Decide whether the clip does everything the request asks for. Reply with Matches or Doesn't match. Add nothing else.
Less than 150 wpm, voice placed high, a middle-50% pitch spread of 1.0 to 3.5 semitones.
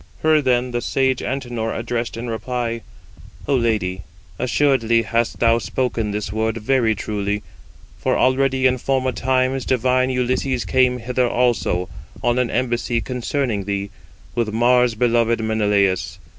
Doesn't match